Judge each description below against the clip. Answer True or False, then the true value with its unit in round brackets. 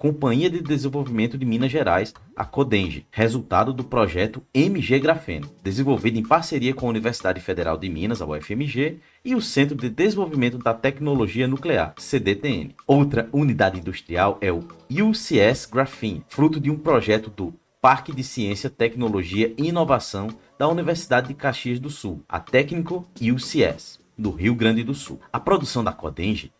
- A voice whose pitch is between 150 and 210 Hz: False (130 Hz)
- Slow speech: False (155 wpm)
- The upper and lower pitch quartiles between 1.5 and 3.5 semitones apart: False (4.7 semitones)